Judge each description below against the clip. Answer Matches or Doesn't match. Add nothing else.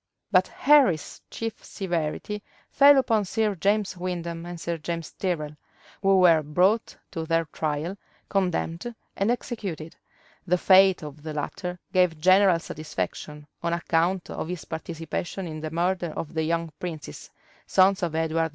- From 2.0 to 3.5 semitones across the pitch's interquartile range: Matches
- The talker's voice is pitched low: Doesn't match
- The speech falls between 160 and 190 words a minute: Doesn't match